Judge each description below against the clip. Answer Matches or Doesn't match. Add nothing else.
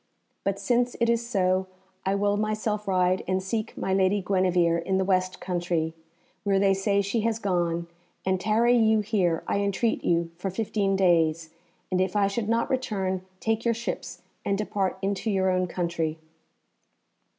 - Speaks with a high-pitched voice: Matches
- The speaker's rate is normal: Matches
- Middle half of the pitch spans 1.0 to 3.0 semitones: Matches